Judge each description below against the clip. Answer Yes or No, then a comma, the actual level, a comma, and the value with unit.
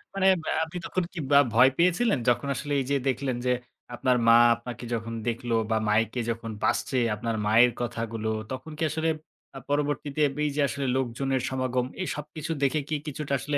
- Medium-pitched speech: No, low, 130 Hz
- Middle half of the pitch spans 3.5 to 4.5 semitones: Yes, average, 4.0 semitones